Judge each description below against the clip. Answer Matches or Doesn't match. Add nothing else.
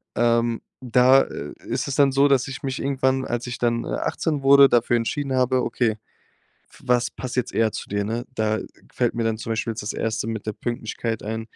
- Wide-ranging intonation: Doesn't match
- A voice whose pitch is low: Matches